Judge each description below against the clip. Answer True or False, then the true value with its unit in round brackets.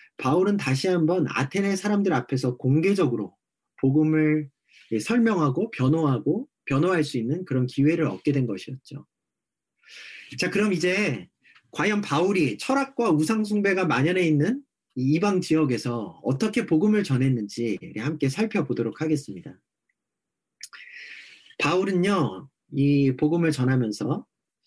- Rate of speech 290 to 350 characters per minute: False (275 characters per minute)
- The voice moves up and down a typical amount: False (6.5 semitones)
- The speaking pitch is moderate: True (155 Hz)